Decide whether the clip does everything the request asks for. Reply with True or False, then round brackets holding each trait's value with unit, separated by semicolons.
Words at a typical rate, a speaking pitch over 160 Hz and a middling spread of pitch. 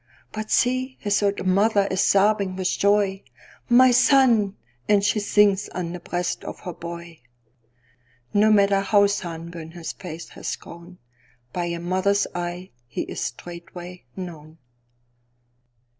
False (120 wpm; 185 Hz; 3.3 semitones)